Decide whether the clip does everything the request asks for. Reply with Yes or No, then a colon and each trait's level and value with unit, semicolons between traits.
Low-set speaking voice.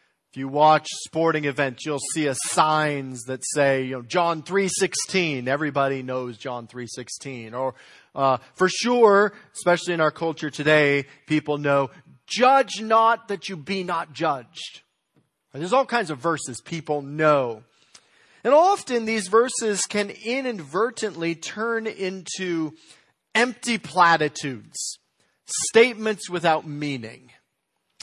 No: medium, 160 Hz